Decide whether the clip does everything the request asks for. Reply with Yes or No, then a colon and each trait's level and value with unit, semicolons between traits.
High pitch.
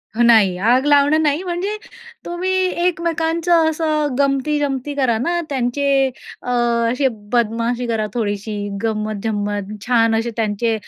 Yes: very high, 250 Hz